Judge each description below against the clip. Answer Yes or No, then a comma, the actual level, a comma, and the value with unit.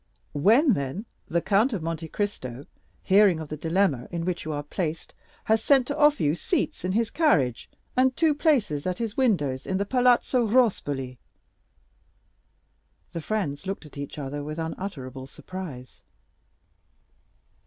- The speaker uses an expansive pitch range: Yes, wide, 7.3 semitones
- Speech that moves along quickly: No, average, 150 wpm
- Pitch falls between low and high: Yes, medium, 180 Hz